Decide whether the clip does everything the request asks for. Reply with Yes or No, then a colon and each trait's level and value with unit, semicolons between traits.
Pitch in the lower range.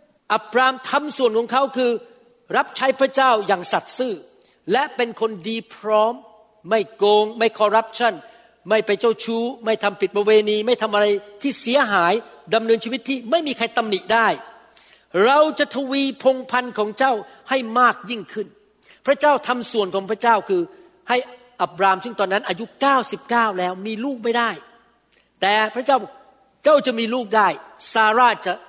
No: high, 230 Hz